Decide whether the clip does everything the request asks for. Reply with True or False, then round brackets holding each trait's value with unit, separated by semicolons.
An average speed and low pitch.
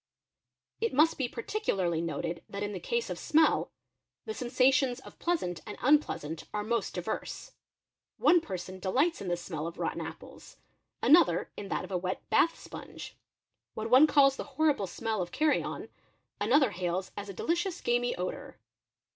False (170 wpm; 230 Hz)